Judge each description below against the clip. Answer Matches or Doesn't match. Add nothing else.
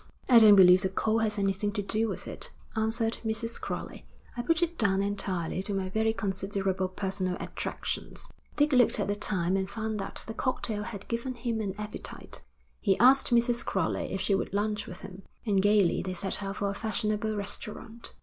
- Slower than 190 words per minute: Doesn't match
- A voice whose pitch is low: Doesn't match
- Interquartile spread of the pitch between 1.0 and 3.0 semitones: Matches